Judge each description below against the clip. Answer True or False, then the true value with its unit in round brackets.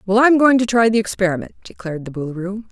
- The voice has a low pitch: False (205 Hz)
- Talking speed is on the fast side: True (220 wpm)